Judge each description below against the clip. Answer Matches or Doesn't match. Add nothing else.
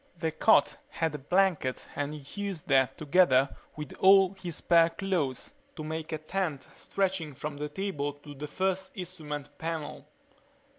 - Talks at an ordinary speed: Matches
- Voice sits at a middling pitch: Matches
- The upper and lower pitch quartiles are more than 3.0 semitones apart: Matches